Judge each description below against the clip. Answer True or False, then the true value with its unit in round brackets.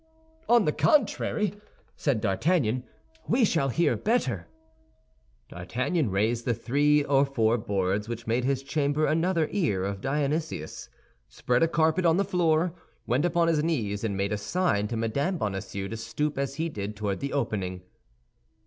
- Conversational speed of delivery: True (155 wpm)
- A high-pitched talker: False (135 Hz)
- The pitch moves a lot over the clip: True (7.4 semitones)